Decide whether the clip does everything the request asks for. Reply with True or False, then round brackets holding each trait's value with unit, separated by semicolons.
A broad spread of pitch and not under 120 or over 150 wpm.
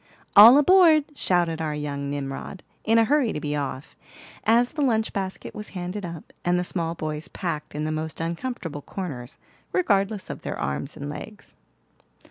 False (6.5 semitones; 170 wpm)